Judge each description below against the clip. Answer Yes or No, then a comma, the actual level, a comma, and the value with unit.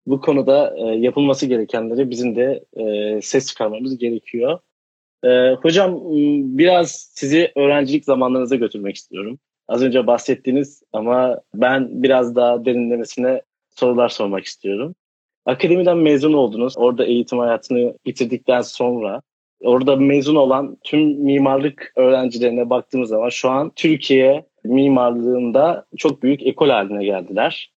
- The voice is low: Yes, low, 130 Hz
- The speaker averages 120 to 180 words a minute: No, average, 110 wpm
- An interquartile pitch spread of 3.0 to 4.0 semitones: No, narrow, 2.4 semitones